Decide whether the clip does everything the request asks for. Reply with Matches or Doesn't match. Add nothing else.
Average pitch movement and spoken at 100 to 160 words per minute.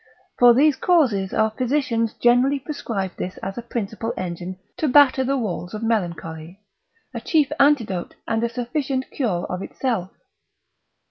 Doesn't match